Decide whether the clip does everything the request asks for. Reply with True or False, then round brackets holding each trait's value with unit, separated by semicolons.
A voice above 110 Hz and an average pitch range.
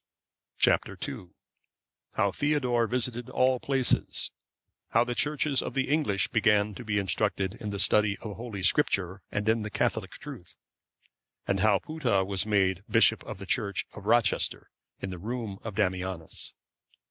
False (105 Hz; 3.7 semitones)